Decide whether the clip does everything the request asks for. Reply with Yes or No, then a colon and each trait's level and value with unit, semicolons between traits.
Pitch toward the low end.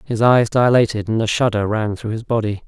Yes: low, 110 Hz